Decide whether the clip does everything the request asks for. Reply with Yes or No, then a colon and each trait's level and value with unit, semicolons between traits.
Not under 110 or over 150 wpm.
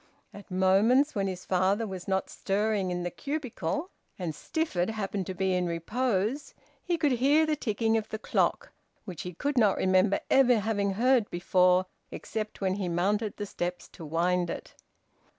No: average, 170 wpm